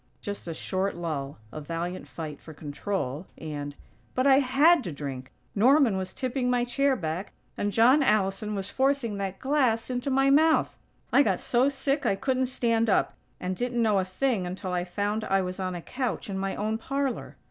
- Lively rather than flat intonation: Yes, wide, 6.2 semitones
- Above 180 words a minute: Yes, average, 195 wpm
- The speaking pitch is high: Yes, high, 210 Hz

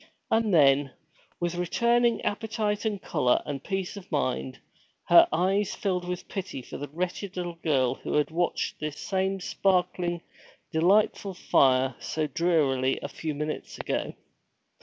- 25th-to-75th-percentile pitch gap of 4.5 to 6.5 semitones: Yes, average, 4.8 semitones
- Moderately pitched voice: Yes, medium, 175 Hz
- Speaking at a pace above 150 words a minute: No, average, 140 wpm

